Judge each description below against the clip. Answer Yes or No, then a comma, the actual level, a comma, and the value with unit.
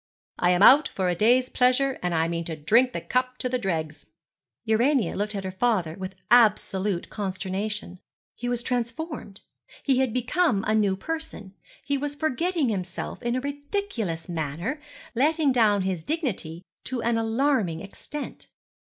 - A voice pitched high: Yes, high, 225 Hz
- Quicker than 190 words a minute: No, average, 160 wpm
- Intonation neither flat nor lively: No, wide, 5.7 semitones